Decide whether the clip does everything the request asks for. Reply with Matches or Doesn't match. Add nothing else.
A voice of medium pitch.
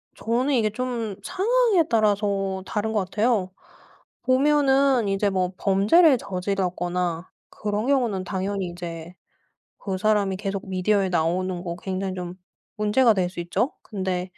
Doesn't match